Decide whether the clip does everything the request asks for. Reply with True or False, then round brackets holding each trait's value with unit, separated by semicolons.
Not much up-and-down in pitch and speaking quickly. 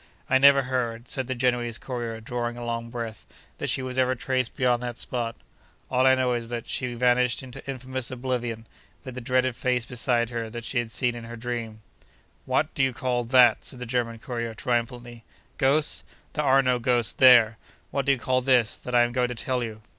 True (1.5 semitones; 210 wpm)